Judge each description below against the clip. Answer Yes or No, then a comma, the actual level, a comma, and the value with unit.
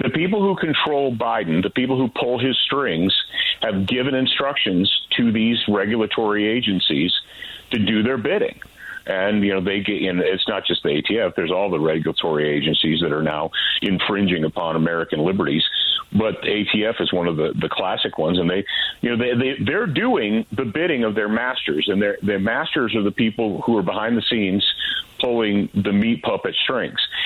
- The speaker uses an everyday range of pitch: Yes, average, 4.1 semitones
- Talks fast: No, average, 185 wpm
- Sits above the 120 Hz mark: No, low, 110 Hz